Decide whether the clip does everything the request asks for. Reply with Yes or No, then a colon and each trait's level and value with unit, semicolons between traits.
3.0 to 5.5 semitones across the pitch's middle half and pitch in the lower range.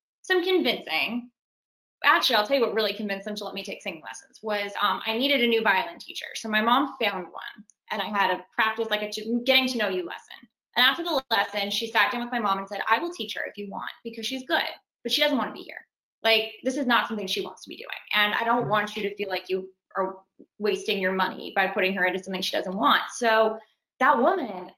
No: average, 3.5 semitones; high, 220 Hz